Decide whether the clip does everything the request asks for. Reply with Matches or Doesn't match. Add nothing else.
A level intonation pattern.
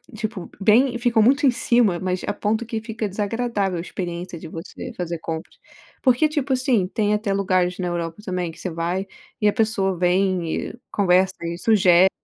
Doesn't match